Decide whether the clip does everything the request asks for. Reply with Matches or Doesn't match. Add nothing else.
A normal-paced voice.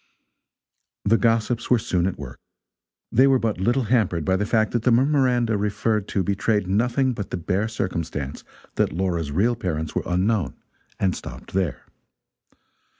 Matches